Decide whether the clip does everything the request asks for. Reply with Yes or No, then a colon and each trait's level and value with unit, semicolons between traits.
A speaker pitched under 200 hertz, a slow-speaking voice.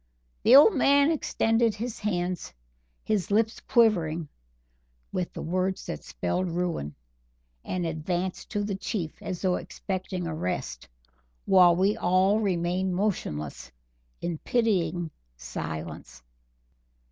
Yes: medium, 185 Hz; slow, 110 wpm